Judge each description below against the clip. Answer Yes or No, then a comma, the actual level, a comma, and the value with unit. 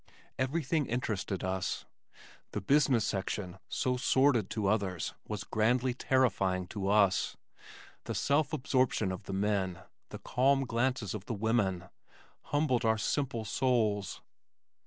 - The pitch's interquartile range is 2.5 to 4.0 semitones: No, average, 4.9 semitones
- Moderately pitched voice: No, low, 110 Hz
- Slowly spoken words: Yes, slow, 125 wpm